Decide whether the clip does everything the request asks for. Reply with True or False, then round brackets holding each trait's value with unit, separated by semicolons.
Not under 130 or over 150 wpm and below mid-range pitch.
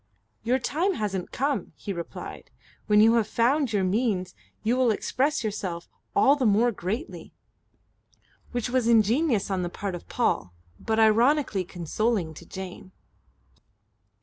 False (140 wpm; 220 Hz)